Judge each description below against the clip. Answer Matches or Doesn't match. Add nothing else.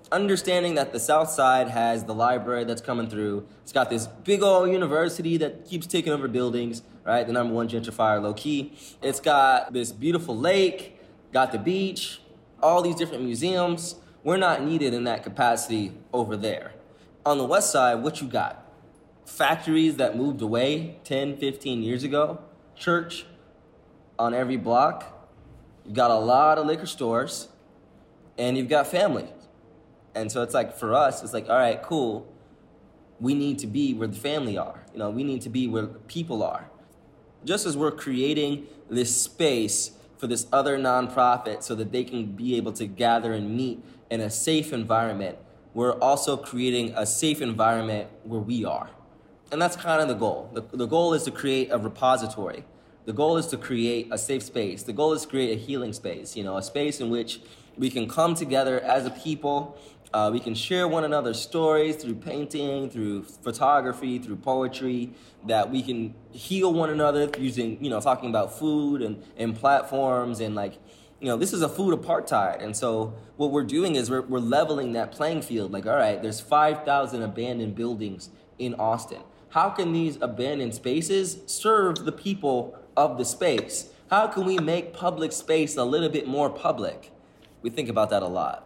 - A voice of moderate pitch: Doesn't match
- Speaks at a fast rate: Doesn't match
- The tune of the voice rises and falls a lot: Doesn't match